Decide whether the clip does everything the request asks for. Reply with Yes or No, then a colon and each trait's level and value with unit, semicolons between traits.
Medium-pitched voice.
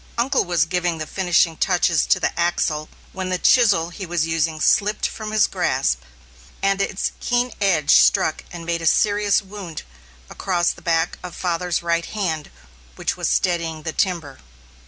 Yes: medium, 175 Hz